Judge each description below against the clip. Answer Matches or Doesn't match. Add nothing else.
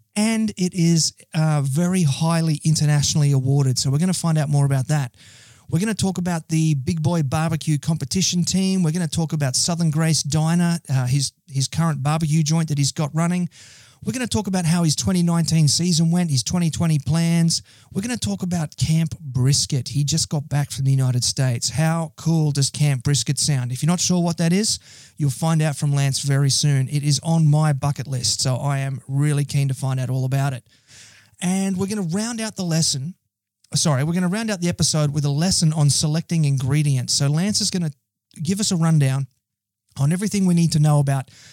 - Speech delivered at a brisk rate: Matches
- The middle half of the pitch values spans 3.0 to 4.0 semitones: Matches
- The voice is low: Doesn't match